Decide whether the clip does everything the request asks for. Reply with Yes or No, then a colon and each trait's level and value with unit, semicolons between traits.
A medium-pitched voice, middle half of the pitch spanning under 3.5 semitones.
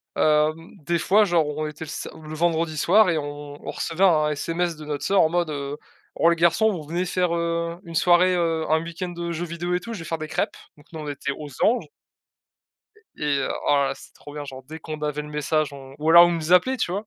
Yes: medium, 165 Hz; narrow, 2.4 semitones